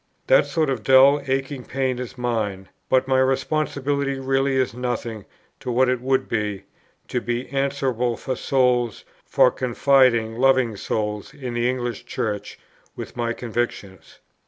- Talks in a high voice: No, low, 125 Hz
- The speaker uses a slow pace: No, average, 145 wpm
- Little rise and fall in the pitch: Yes, narrow, 2.3 semitones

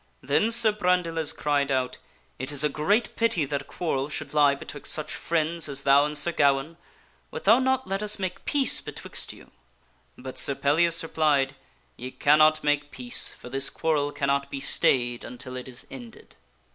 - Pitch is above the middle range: No, medium, 145 Hz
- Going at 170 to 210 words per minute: Yes, average, 190 wpm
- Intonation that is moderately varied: Yes, average, 3.6 semitones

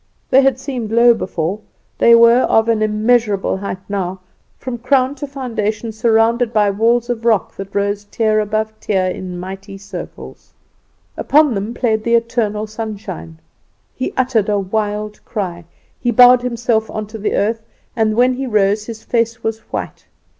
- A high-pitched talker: Yes, high, 220 Hz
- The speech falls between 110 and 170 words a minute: Yes, average, 160 wpm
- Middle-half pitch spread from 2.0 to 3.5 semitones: Yes, narrow, 2.6 semitones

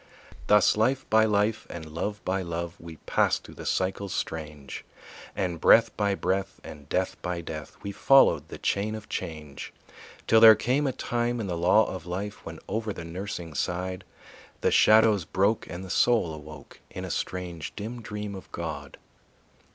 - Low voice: Yes, very low, 95 Hz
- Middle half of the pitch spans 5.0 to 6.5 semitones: No, average, 4.3 semitones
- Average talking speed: Yes, average, 175 wpm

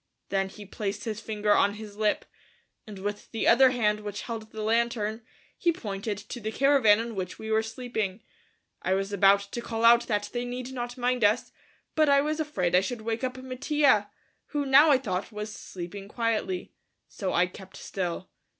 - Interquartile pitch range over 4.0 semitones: No, average, 3.4 semitones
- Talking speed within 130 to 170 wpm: No, average, 190 wpm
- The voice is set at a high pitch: Yes, high, 220 Hz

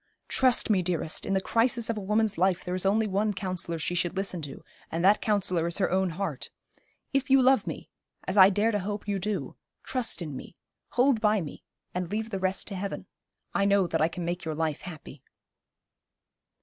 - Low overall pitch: No, high, 190 Hz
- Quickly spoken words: Yes, fast, 210 wpm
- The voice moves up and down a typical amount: Yes, average, 3.3 semitones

